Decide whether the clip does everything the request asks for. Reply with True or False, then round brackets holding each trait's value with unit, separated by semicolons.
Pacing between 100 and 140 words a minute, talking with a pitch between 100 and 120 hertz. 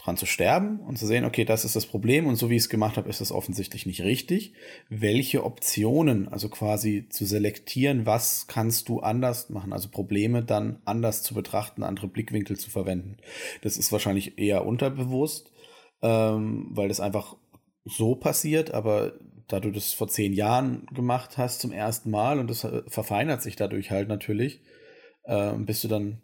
False (180 wpm; 110 Hz)